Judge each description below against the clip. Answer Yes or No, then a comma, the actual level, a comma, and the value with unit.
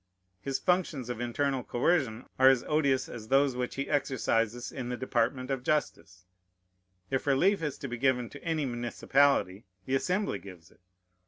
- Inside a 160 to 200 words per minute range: Yes, average, 165 wpm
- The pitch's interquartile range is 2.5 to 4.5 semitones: Yes, average, 2.9 semitones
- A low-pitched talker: Yes, low, 130 Hz